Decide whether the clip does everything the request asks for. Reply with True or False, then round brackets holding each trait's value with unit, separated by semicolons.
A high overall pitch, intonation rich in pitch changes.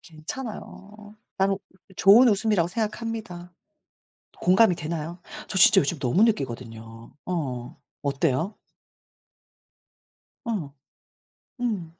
False (180 Hz; 6.0 semitones)